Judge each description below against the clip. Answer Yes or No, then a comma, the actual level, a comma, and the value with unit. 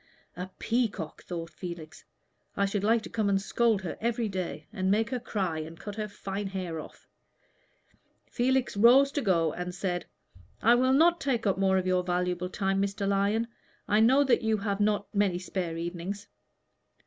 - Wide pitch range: No, average, 3.7 semitones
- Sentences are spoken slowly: No, average, 185 wpm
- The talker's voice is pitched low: No, high, 200 Hz